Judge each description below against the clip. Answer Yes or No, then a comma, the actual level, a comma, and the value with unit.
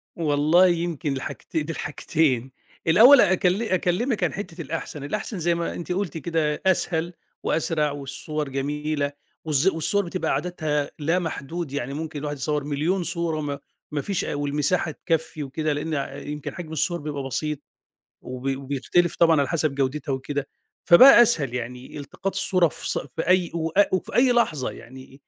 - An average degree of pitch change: Yes, average, 3.4 semitones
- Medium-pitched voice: Yes, medium, 155 Hz